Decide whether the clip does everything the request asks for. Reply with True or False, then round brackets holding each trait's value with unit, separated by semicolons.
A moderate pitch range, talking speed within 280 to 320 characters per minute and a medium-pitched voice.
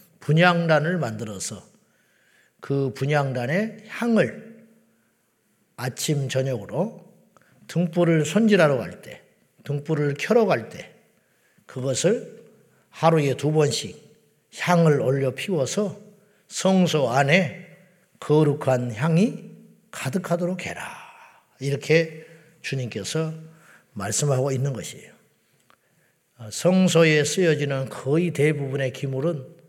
False (4.6 semitones; 205 characters per minute; 155 Hz)